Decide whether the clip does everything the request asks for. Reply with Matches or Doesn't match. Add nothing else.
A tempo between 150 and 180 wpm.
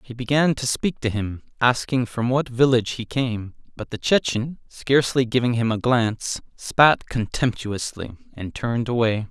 Matches